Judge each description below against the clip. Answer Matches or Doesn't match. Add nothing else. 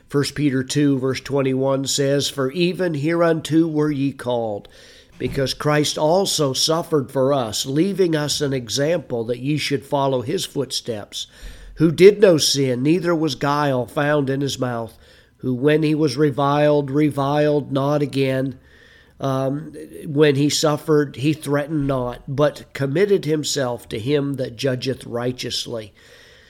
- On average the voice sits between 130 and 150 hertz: Matches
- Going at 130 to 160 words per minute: Matches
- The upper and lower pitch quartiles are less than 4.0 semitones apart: Matches